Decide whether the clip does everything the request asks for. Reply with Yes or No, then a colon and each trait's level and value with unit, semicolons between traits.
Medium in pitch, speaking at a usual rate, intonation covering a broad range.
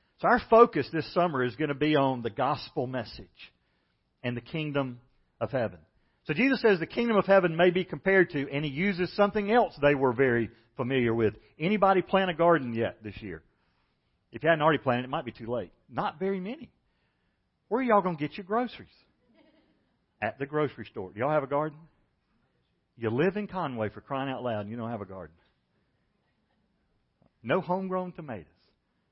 Yes: medium, 145 Hz; average, 190 wpm; wide, 7.7 semitones